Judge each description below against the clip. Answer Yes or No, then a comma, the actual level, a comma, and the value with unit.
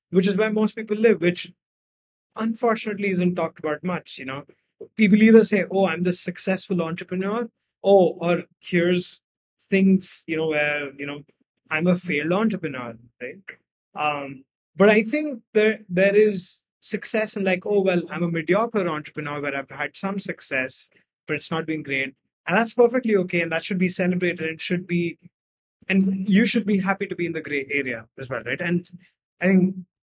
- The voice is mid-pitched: Yes, medium, 180 Hz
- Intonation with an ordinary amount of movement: Yes, average, 4.5 semitones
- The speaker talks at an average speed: Yes, average, 180 wpm